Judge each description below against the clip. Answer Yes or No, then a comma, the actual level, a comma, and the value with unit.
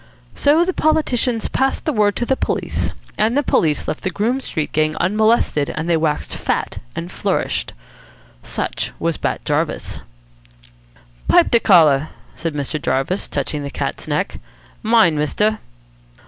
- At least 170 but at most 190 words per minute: No, average, 145 wpm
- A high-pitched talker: No, medium, 180 Hz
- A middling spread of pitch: No, wide, 7.4 semitones